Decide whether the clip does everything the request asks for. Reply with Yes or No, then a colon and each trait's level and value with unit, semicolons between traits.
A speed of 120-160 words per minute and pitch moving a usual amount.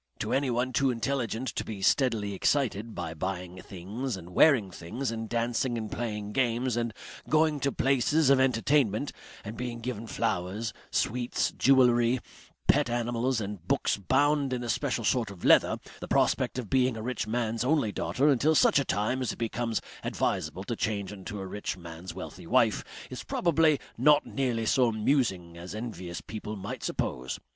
No: average, 170 wpm; average, 4.0 semitones